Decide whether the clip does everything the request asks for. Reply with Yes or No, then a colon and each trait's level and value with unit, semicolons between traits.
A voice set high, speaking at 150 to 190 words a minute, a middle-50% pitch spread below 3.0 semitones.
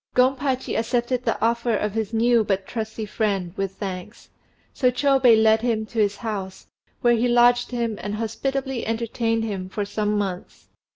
Yes: high, 225 Hz; average, 165 wpm; narrow, 2.6 semitones